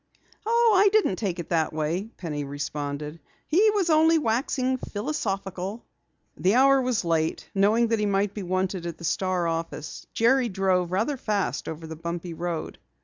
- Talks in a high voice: Yes, high, 195 Hz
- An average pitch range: No, wide, 6.7 semitones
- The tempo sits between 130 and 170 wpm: Yes, average, 165 wpm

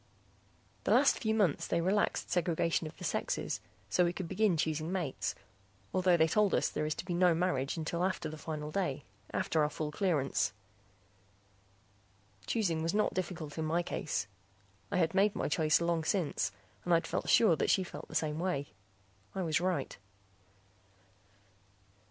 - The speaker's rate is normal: Yes, average, 170 wpm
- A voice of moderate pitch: Yes, medium, 170 Hz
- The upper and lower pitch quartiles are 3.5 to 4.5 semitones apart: No, average, 3.0 semitones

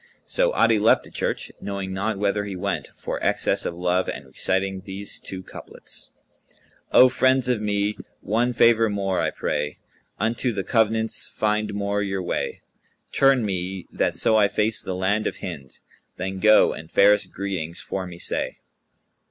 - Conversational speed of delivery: Yes, average, 170 wpm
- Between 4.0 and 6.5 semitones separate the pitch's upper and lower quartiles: No, narrow, 2.6 semitones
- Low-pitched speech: Yes, low, 100 Hz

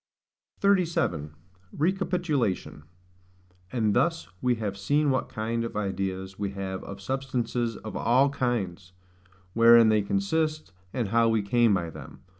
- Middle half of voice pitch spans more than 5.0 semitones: Yes, wide, 5.5 semitones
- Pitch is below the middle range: Yes, low, 115 Hz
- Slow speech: Yes, slow, 130 wpm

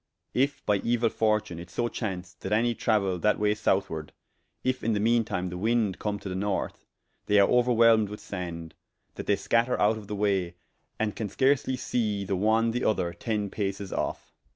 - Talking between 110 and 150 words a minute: No, average, 195 wpm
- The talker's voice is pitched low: Yes, low, 105 Hz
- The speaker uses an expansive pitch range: No, average, 3.1 semitones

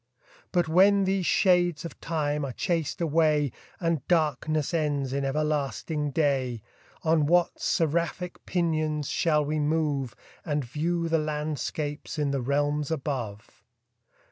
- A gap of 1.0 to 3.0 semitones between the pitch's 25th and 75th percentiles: Yes, narrow, 2.4 semitones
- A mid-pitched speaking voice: Yes, medium, 150 Hz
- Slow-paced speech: Yes, slow, 125 wpm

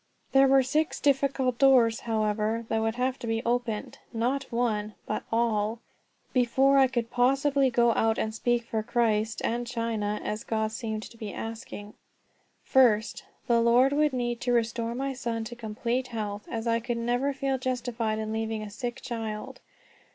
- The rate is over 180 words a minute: No, average, 170 wpm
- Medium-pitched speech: No, high, 235 Hz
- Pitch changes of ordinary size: No, narrow, 2.3 semitones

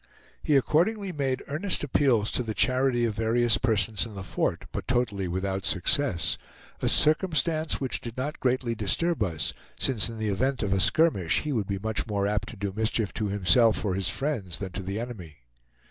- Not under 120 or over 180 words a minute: No, average, 190 wpm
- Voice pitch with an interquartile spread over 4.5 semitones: Yes, average, 5.2 semitones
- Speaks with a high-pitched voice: No, low, 115 Hz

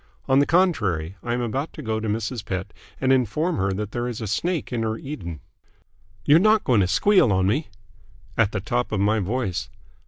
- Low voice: Yes, low, 115 Hz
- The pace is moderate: No, fast, 210 wpm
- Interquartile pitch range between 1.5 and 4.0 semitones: No, average, 5.3 semitones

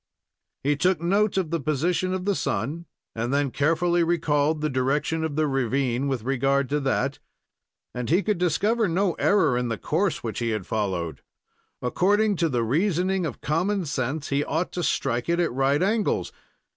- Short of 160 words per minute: No, average, 180 wpm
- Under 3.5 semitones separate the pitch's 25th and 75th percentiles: No, average, 5.1 semitones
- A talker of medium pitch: Yes, medium, 155 Hz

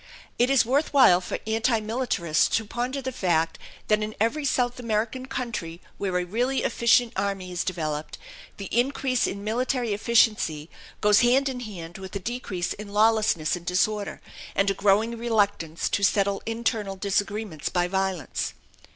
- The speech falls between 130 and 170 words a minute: Yes, average, 160 wpm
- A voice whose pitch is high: Yes, high, 210 Hz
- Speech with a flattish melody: No, average, 4.2 semitones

